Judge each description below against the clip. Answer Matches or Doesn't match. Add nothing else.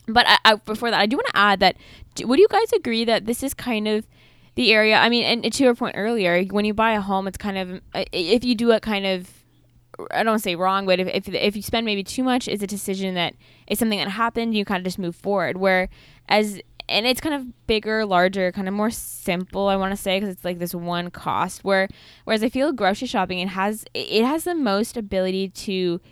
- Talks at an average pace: Doesn't match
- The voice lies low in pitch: Doesn't match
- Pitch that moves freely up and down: Doesn't match